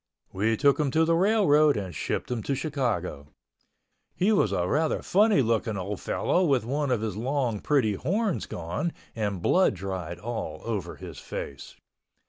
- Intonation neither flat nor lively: No, wide, 7.5 semitones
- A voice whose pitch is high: No, low, 120 Hz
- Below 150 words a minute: No, average, 165 wpm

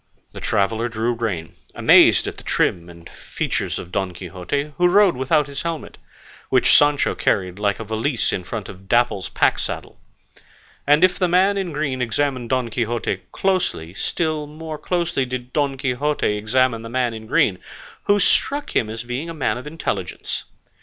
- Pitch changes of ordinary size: No, wide, 5.7 semitones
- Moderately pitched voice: No, low, 125 Hz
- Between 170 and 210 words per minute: Yes, average, 175 wpm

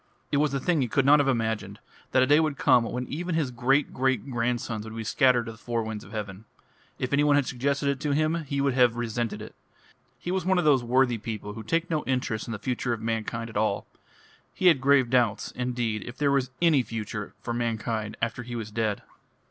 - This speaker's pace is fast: Yes, fast, 235 wpm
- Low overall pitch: Yes, low, 125 Hz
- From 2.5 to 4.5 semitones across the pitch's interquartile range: Yes, average, 3.7 semitones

